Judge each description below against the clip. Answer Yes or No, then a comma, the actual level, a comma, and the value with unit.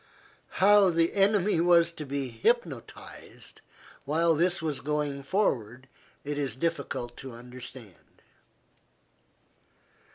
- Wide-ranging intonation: No, average, 4.8 semitones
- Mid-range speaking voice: Yes, medium, 150 Hz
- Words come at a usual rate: No, slow, 100 wpm